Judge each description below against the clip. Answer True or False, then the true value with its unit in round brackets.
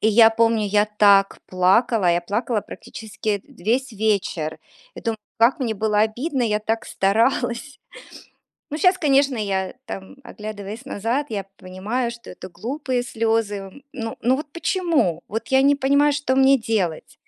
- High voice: True (225 Hz)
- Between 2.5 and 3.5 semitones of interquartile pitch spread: False (4.3 semitones)